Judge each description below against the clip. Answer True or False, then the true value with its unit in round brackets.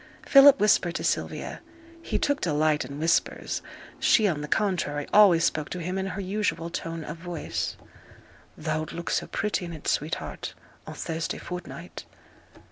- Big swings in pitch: False (3.6 semitones)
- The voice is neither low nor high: True (170 Hz)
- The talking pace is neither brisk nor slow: True (155 wpm)